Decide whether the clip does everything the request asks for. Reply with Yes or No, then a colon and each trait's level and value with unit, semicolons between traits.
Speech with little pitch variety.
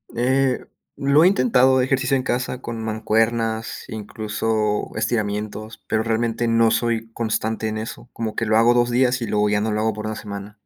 Yes: narrow, 2.0 semitones